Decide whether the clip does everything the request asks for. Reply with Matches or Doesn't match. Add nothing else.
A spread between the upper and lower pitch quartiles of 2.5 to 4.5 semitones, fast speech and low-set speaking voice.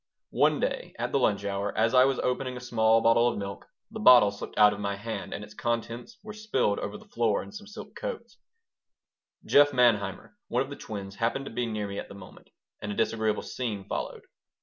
Matches